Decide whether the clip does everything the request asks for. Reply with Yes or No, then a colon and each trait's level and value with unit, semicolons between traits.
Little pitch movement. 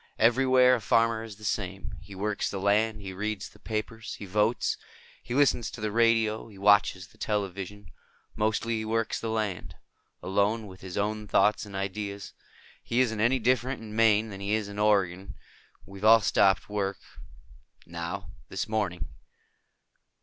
Yes: narrow, 2.2 semitones